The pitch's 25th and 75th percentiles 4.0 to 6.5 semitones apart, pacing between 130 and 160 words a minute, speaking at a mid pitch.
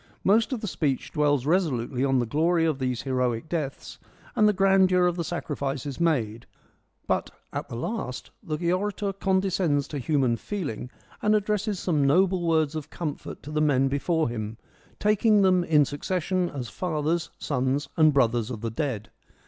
No: wide, 5.5 semitones; average, 170 wpm; medium, 155 Hz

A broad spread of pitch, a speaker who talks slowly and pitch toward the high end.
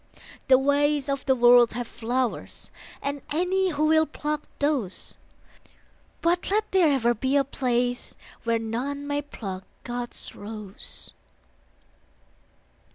No: average, 3.6 semitones; slow, 120 wpm; very high, 270 Hz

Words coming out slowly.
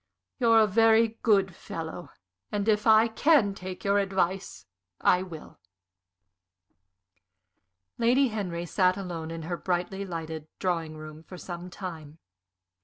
Yes: slow, 125 wpm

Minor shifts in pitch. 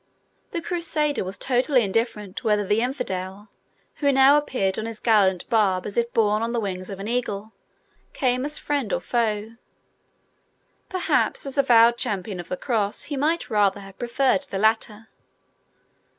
No: average, 4.3 semitones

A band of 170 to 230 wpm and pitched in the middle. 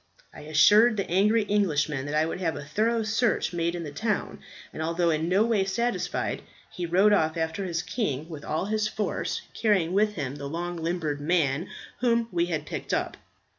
Yes: average, 195 wpm; medium, 175 Hz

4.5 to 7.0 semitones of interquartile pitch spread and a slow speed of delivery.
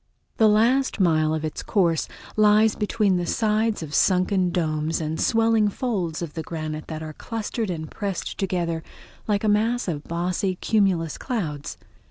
No: average, 4.9 semitones; average, 160 wpm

